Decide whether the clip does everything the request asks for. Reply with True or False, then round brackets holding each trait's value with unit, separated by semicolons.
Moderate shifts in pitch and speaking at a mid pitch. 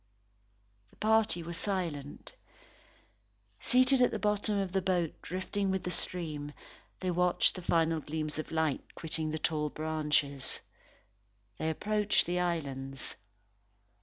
True (3.7 semitones; 170 Hz)